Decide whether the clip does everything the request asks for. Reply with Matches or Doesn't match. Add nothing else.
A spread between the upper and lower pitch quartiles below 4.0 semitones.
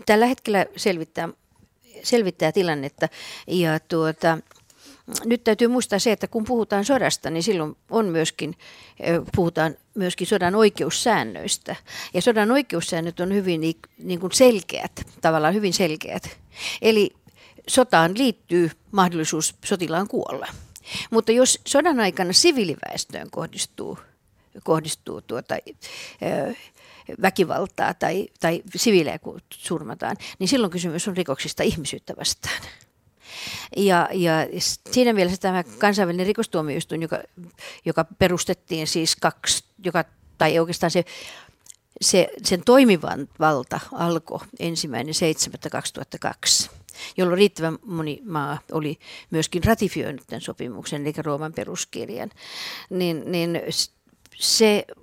Doesn't match